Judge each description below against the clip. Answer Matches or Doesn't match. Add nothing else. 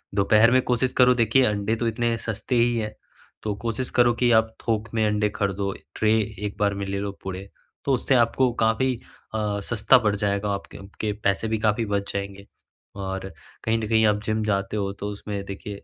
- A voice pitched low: Matches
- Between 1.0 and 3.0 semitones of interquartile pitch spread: Matches